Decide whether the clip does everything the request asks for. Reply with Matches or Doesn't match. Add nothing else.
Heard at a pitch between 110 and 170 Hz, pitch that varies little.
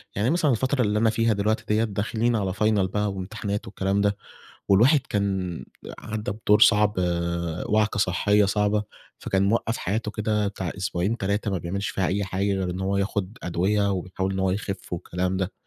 Doesn't match